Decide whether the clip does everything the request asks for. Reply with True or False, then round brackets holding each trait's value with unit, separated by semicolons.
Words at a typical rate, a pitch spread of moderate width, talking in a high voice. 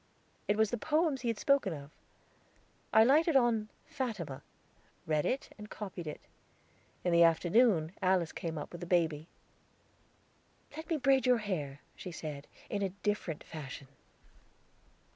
False (145 wpm; 7.1 semitones; 195 Hz)